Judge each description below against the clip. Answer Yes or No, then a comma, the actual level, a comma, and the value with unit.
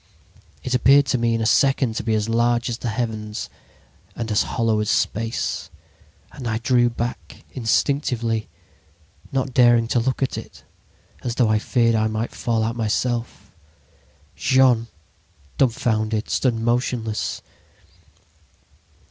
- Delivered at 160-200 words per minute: No, slow, 135 wpm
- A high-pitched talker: No, low, 115 Hz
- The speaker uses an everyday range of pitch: No, narrow, 1.9 semitones